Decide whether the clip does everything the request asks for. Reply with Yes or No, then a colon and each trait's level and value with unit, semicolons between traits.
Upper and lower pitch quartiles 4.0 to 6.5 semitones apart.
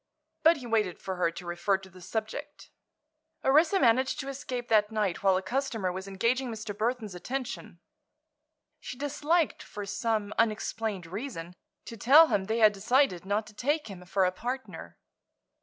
Yes: average, 5.2 semitones